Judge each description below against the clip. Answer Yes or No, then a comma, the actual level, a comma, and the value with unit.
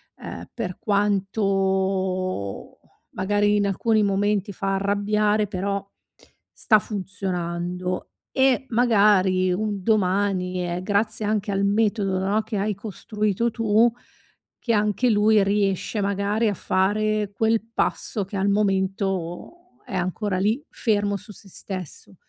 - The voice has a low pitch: No, high, 200 Hz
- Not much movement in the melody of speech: Yes, narrow, 1.9 semitones